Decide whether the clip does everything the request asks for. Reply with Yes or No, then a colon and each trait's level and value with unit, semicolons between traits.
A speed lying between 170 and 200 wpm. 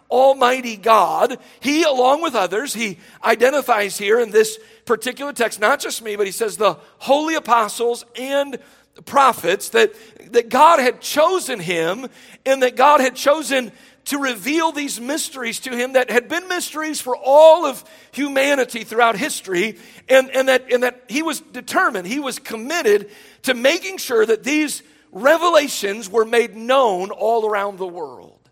No: average, 160 wpm